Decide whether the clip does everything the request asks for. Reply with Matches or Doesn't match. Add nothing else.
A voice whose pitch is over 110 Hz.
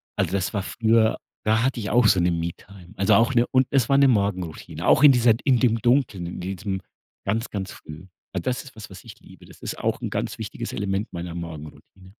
Doesn't match